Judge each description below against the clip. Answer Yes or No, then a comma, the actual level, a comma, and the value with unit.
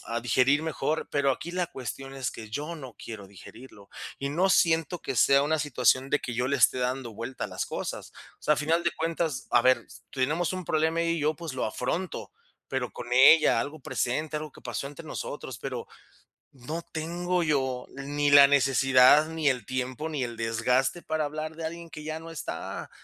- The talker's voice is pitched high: No, medium, 145 Hz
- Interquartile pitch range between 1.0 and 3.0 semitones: No, average, 3.8 semitones